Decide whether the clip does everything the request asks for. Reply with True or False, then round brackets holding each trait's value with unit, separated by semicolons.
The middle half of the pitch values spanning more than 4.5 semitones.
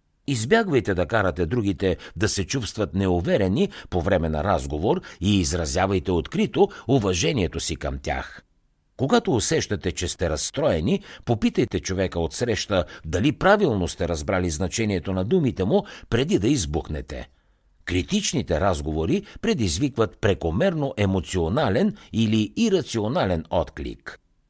True (5.3 semitones)